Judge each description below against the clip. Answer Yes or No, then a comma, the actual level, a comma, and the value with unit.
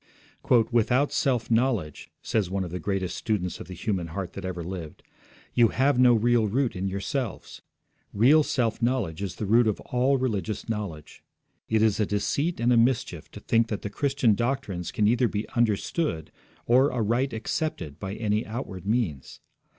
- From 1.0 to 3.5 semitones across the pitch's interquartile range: No, average, 4.3 semitones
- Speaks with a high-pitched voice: No, low, 110 Hz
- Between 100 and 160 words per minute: No, average, 175 wpm